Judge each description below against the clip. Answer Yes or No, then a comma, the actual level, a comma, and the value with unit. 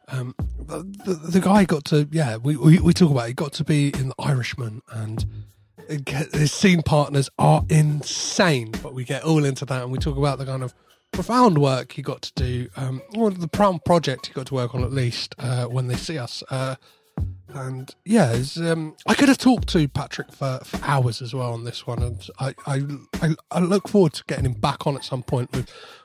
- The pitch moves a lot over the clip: No, average, 4.4 semitones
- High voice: No, medium, 140 Hz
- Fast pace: Yes, fast, 230 wpm